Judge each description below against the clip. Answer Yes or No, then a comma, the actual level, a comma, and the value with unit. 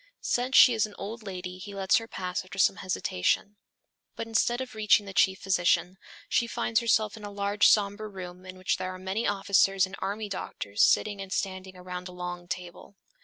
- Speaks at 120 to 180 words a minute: No, average, 200 wpm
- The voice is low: No, high, 195 Hz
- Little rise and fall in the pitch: Yes, narrow, 2.3 semitones